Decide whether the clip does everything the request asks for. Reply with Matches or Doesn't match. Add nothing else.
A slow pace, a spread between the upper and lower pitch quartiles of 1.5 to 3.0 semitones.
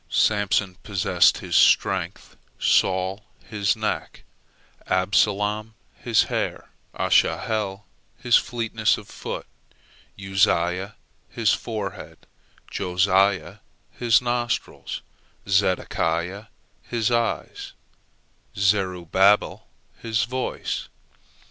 Matches